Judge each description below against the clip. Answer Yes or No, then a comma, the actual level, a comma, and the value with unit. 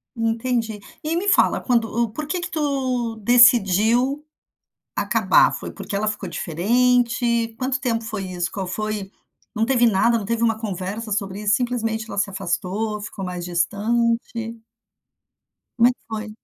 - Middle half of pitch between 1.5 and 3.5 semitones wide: Yes, average, 2.9 semitones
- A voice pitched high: Yes, high, 225 Hz